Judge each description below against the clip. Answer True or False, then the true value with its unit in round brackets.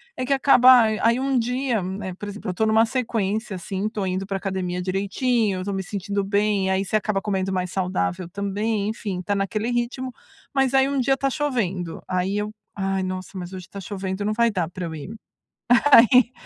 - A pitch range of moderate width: True (3.7 semitones)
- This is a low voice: False (200 Hz)